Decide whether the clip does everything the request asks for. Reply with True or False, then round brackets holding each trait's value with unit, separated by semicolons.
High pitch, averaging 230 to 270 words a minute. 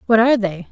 True (215 Hz; 250 wpm)